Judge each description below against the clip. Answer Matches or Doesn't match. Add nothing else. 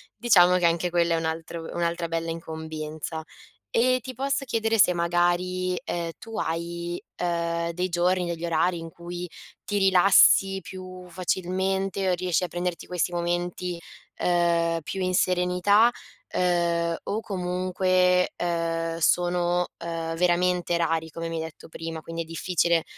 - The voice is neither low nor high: Matches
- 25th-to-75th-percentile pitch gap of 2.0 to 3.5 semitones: Doesn't match